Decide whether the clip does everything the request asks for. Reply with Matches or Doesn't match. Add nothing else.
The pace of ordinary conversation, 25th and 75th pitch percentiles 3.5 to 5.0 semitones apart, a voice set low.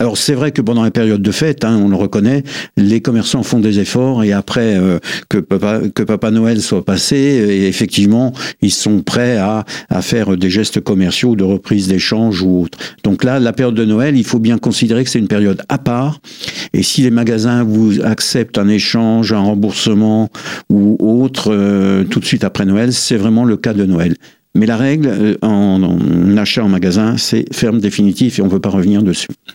Doesn't match